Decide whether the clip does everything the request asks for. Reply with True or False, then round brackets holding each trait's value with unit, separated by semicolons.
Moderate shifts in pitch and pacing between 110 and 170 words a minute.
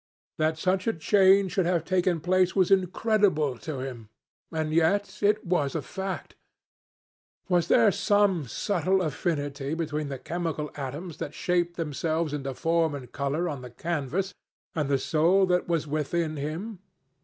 True (4.0 semitones; 155 wpm)